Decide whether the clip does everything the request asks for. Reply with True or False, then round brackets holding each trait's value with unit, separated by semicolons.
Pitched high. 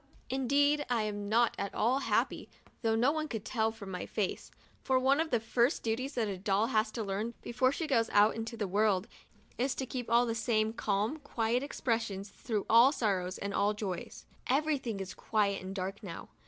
True (225 Hz)